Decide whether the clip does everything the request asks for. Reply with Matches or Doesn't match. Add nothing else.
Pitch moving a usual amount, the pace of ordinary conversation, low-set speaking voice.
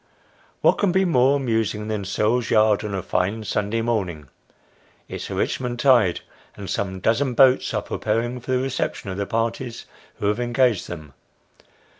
Matches